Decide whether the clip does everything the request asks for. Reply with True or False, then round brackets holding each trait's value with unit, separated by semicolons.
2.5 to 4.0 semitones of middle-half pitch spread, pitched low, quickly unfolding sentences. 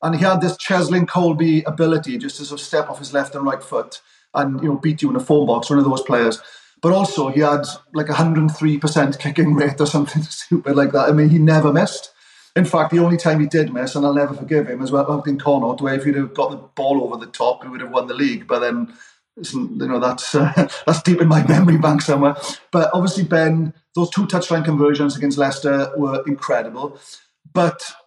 False (3.1 semitones; 155 Hz; 235 wpm)